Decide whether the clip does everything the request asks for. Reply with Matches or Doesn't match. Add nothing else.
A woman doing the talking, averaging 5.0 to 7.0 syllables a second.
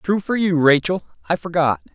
Doesn't match